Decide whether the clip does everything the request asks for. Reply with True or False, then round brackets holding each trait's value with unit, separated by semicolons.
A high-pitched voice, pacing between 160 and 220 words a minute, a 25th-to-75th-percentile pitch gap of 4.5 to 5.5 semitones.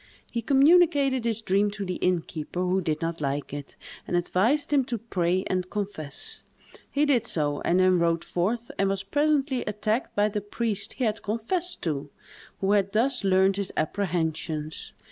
True (200 Hz; 170 wpm; 5.1 semitones)